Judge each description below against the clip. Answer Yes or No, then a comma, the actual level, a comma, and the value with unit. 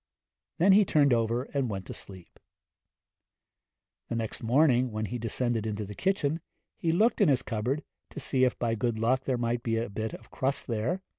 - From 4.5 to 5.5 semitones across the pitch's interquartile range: No, average, 3.9 semitones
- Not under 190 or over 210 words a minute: Yes, average, 195 wpm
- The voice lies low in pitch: Yes, low, 120 Hz